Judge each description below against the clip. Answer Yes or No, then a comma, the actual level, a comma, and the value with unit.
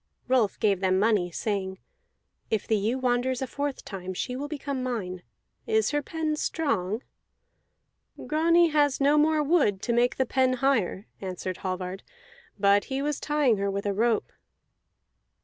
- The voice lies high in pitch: Yes, high, 245 Hz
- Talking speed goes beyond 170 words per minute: No, average, 155 wpm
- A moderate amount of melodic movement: No, wide, 6.4 semitones